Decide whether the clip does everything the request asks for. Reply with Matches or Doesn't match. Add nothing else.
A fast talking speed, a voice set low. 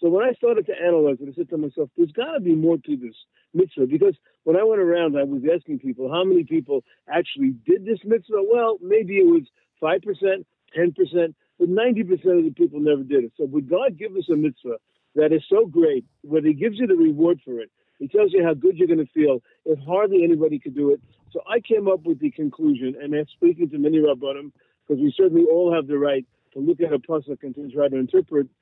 Doesn't match